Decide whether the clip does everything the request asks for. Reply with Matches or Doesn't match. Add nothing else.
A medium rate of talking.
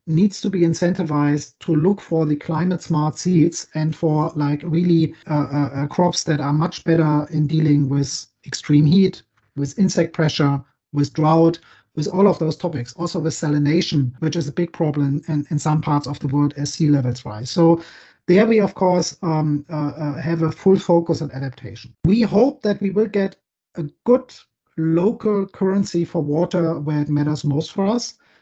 Matches